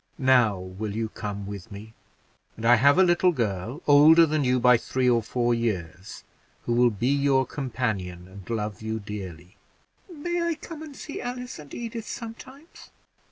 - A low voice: Yes, low, 120 Hz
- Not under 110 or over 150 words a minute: No, average, 170 wpm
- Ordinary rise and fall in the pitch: No, wide, 7.4 semitones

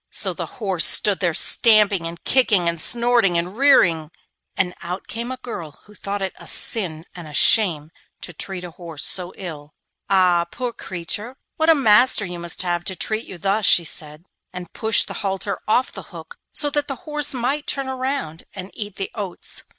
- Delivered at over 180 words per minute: Yes, average, 195 wpm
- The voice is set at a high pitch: Yes, high, 195 Hz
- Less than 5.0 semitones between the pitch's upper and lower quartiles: No, wide, 5.4 semitones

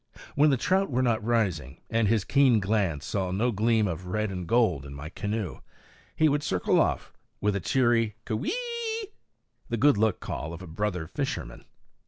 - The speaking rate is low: No, average, 180 wpm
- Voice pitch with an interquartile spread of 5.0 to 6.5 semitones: Yes, average, 5.3 semitones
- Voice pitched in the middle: No, low, 110 Hz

